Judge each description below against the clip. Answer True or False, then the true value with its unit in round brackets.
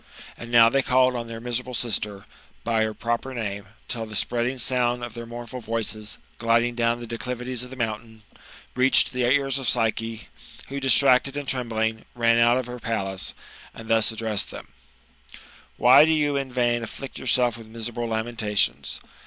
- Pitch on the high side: False (120 Hz)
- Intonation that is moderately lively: False (2.0 semitones)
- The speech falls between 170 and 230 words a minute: True (175 wpm)